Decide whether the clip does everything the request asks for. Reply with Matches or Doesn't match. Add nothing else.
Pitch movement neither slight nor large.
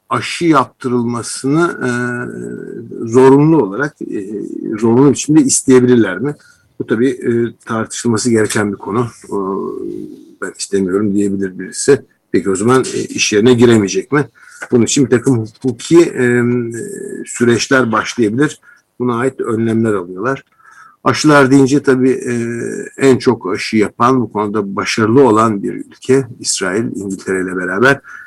Matches